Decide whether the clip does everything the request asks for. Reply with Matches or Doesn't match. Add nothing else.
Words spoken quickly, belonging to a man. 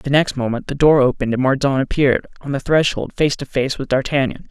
Matches